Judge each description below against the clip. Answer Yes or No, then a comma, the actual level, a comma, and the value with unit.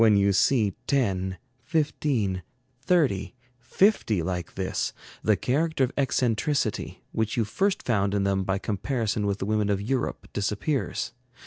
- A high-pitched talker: No, low, 110 Hz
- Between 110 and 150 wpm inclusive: Yes, average, 140 wpm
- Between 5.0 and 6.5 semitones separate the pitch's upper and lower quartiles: Yes, average, 5.3 semitones